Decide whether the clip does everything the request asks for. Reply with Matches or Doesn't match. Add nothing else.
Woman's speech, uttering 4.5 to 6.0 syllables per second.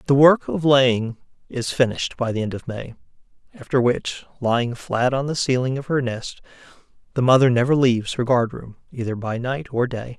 Doesn't match